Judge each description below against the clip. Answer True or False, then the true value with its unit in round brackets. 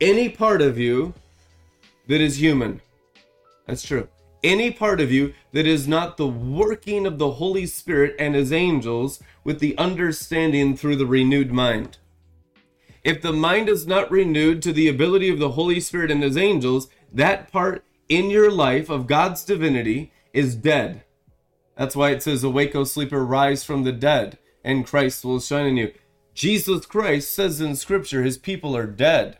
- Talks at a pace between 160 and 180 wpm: True (170 wpm)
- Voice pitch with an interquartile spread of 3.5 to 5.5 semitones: True (4.9 semitones)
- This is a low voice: False (145 Hz)